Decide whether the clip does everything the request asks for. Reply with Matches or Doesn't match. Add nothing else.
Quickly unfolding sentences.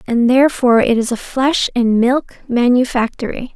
Doesn't match